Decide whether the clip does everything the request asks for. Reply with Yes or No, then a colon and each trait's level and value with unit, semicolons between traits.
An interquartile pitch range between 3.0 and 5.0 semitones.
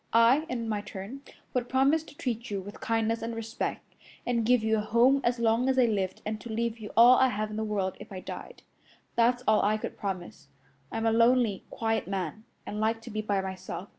No: narrow, 2.4 semitones